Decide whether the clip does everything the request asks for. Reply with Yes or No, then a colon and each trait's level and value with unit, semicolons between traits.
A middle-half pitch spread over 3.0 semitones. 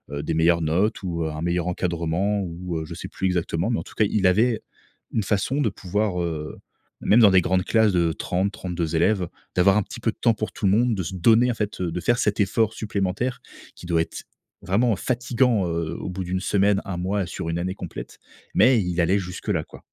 Yes: average, 3.6 semitones